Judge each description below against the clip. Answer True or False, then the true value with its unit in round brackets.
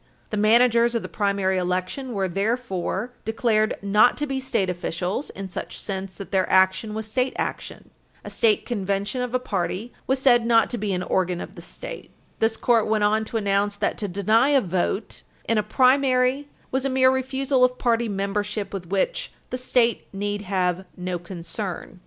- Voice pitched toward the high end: True (215 Hz)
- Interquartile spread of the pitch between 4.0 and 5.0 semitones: True (4.4 semitones)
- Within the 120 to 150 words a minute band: False (190 wpm)